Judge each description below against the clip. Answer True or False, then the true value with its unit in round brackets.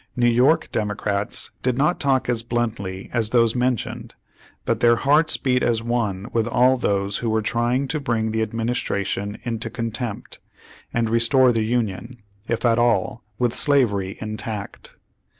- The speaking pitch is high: False (115 Hz)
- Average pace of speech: True (160 wpm)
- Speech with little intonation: True (2.2 semitones)